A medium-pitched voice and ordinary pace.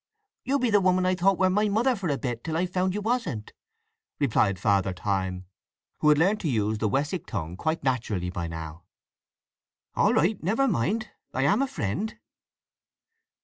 Yes: medium, 155 Hz; average, 180 wpm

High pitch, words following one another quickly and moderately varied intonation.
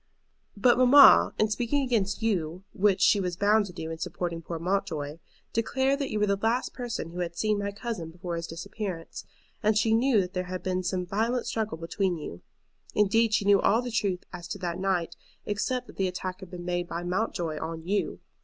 Yes: high, 195 Hz; fast, 210 wpm; average, 4.0 semitones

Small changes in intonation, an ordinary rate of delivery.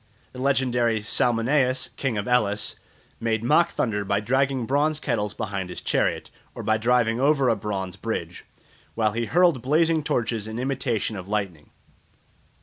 No: average, 4.1 semitones; average, 150 wpm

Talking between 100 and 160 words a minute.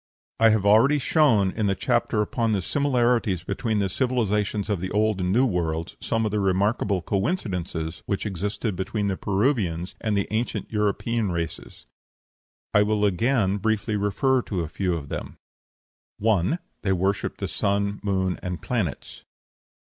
Yes: average, 155 wpm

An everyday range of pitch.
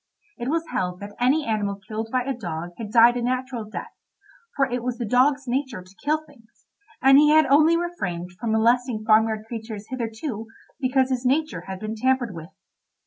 Yes: average, 3.7 semitones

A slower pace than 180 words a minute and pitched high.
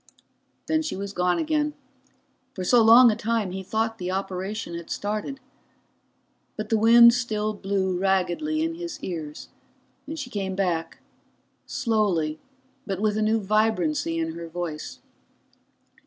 Yes: average, 140 wpm; high, 210 Hz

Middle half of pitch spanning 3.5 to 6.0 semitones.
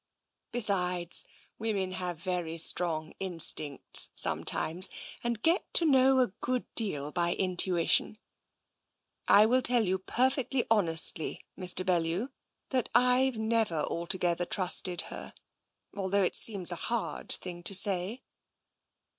Yes: average, 4.9 semitones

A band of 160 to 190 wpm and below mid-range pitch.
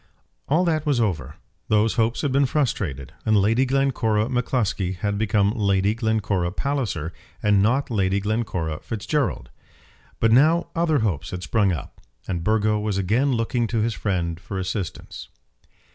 No: average, 150 wpm; low, 110 Hz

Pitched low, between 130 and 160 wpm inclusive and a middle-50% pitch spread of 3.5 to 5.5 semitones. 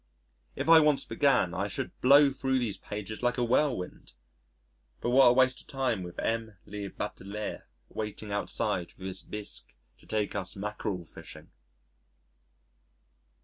Yes: low, 110 Hz; average, 145 wpm; average, 4.4 semitones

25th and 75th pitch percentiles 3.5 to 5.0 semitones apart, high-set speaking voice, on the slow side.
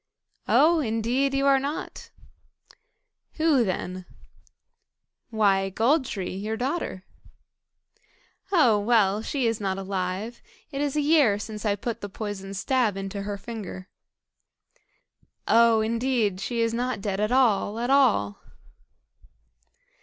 Yes: average, 4.5 semitones; high, 225 Hz; slow, 125 wpm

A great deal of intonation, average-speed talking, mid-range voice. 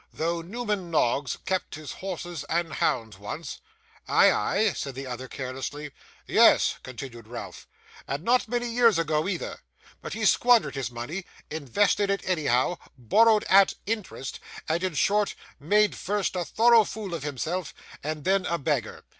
Yes: wide, 6.5 semitones; average, 155 wpm; medium, 170 Hz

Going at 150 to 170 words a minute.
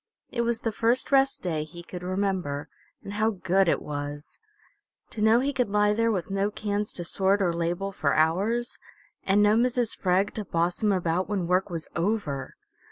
No: average, 190 wpm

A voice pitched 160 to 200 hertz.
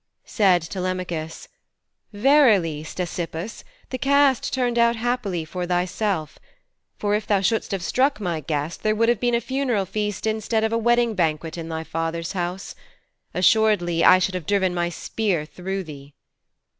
Yes: high, 190 Hz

